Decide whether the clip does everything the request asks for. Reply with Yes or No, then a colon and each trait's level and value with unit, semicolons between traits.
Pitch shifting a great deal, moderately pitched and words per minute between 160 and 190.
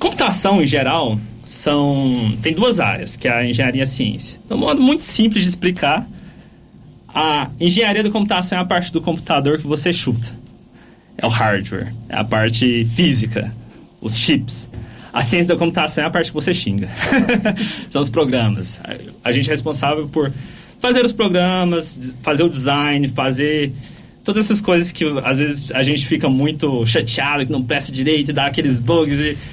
Yes: wide, 5.7 semitones; medium, 145 Hz; average, 175 wpm